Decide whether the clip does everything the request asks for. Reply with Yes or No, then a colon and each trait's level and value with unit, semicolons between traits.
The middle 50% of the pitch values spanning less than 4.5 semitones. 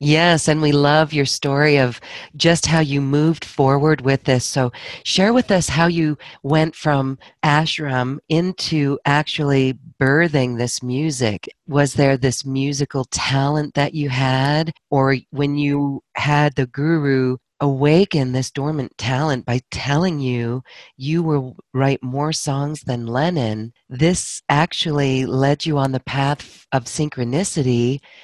Yes: narrow, 2.5 semitones